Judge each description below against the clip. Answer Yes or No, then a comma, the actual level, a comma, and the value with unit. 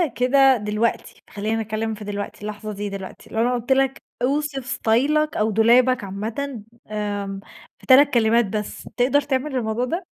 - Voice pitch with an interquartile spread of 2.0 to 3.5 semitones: No, average, 3.9 semitones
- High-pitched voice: Yes, high, 230 Hz